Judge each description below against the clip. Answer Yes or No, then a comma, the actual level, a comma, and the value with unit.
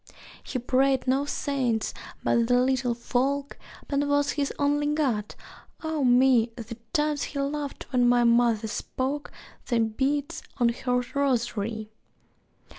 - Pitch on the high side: Yes, very high, 260 Hz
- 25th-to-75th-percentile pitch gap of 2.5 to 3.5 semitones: Yes, average, 3.1 semitones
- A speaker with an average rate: No, slow, 130 wpm